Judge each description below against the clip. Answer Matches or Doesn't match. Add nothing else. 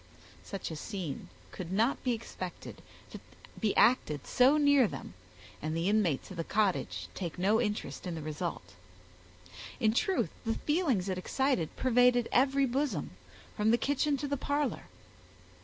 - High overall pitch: Matches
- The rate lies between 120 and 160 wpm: Matches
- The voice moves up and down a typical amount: Doesn't match